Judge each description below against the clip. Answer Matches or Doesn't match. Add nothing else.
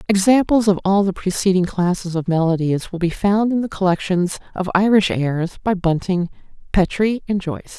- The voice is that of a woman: Matches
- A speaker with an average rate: Matches